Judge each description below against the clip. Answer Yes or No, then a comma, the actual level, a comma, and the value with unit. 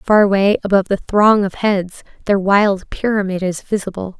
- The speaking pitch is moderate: No, high, 195 Hz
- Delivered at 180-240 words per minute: No, average, 170 wpm